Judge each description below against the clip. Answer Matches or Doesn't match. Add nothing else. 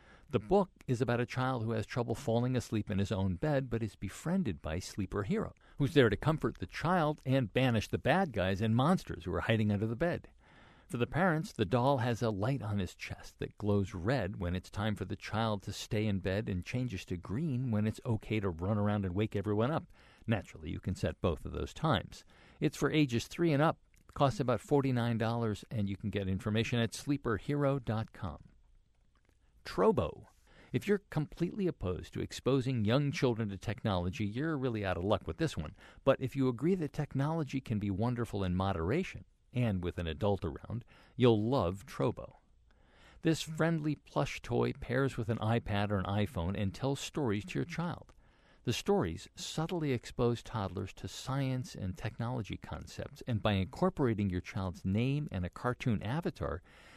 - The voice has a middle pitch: Doesn't match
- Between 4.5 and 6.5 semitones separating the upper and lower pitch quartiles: Matches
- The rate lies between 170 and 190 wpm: Matches